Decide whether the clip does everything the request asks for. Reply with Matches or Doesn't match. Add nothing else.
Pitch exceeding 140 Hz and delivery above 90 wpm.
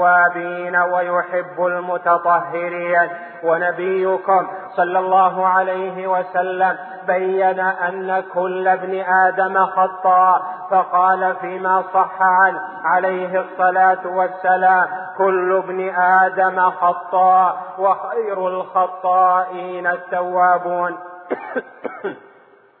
Doesn't match